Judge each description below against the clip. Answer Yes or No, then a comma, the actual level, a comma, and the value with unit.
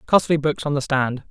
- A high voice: No, medium, 140 Hz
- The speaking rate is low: No, fast, 230 wpm